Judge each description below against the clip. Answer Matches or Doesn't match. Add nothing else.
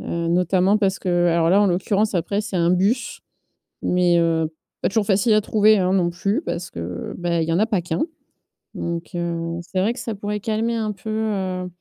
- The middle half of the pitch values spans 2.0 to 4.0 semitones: Matches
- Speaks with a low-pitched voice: Doesn't match